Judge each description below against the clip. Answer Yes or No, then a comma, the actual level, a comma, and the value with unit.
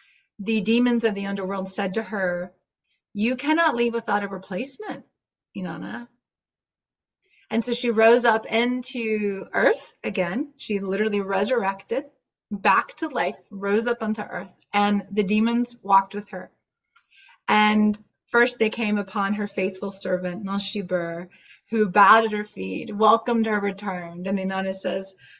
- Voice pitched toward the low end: No, high, 210 Hz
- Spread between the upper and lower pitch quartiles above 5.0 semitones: No, average, 3.0 semitones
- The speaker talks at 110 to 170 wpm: Yes, average, 140 wpm